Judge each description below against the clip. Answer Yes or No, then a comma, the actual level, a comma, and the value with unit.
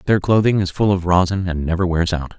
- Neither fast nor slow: No, fast, 250 wpm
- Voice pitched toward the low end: Yes, very low, 90 Hz